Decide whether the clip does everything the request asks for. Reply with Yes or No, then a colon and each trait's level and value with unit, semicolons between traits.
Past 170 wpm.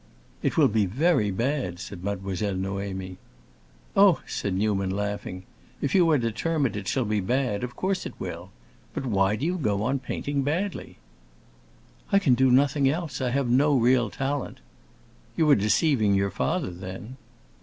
No: average, 165 wpm